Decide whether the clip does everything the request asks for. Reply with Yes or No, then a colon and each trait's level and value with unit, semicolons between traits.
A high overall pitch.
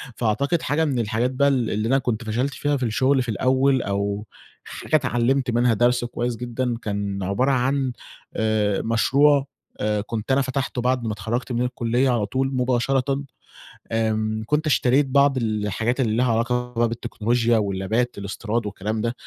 No: low, 120 Hz